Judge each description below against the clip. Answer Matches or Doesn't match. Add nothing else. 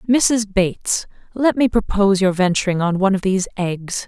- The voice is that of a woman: Matches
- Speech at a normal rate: Matches